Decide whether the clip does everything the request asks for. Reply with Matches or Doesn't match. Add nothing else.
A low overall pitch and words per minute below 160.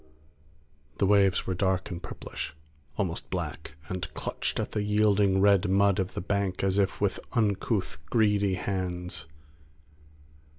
Matches